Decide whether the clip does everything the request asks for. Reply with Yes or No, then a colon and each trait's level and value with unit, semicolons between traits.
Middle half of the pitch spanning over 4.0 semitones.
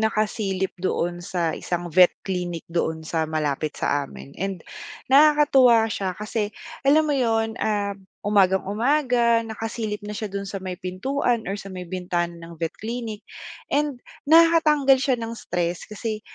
Yes: average, 4.7 semitones